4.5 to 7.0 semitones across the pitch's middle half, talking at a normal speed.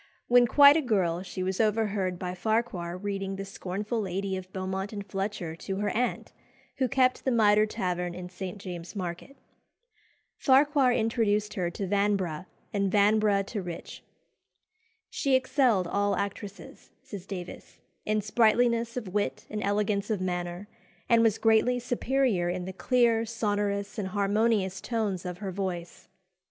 No: average, 3.2 semitones; average, 150 wpm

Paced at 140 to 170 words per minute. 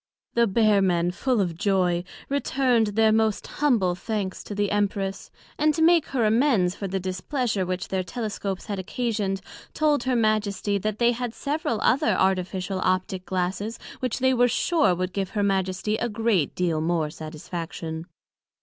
Yes: average, 165 wpm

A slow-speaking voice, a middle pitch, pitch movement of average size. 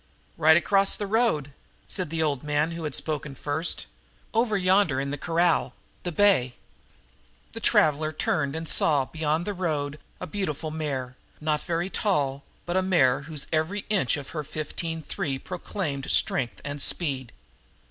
No: average, 155 wpm; medium, 155 Hz; average, 3.7 semitones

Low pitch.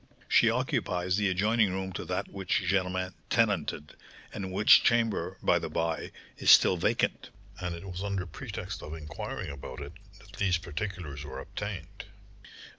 Yes: very low, 95 Hz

